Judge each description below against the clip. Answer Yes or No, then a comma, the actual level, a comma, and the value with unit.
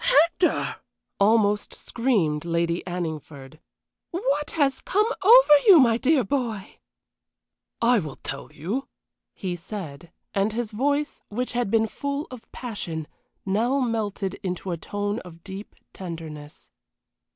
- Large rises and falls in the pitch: Yes, wide, 6.9 semitones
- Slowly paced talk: Yes, slow, 125 wpm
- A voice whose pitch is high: Yes, high, 210 Hz